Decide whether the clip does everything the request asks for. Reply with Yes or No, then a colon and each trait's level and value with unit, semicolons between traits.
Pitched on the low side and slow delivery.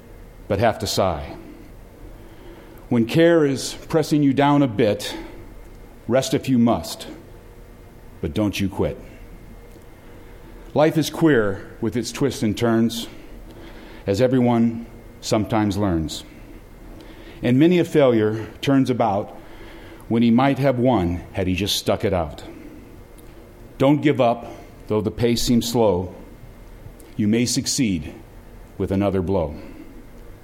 Yes: low, 115 Hz; slow, 125 wpm